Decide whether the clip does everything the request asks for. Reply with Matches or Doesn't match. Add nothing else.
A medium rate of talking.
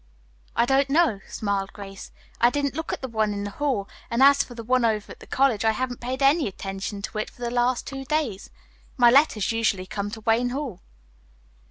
Doesn't match